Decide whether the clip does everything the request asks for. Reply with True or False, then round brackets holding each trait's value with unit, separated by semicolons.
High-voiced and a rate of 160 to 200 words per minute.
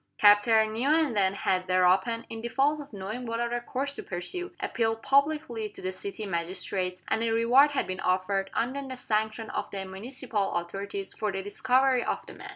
True (220 Hz; 180 wpm)